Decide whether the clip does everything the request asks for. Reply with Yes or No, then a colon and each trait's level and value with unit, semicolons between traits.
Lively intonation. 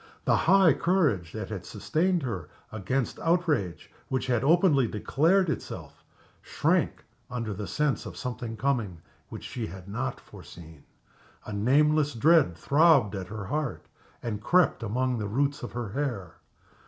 Yes: wide, 6.5 semitones